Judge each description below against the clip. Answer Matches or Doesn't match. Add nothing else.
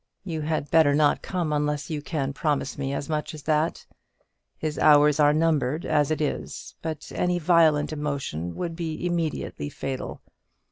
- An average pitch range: Doesn't match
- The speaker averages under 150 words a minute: Doesn't match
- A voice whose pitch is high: Doesn't match